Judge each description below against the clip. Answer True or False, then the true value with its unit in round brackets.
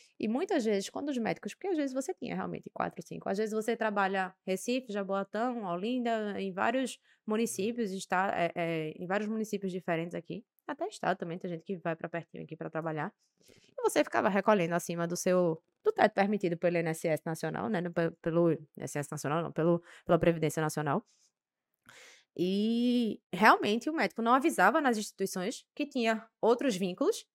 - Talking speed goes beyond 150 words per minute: True (170 wpm)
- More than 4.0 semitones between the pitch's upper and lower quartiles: True (5.2 semitones)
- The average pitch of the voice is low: False (195 Hz)